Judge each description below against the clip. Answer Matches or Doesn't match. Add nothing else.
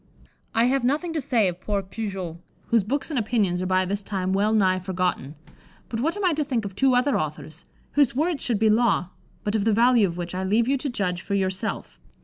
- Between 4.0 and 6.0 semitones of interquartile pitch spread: Matches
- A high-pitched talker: Matches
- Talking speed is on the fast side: Matches